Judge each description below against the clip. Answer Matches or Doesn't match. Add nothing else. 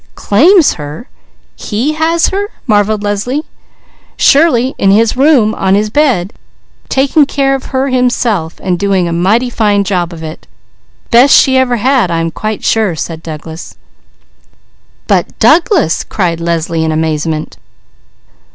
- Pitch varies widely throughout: Matches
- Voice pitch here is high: Matches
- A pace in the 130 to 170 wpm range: Matches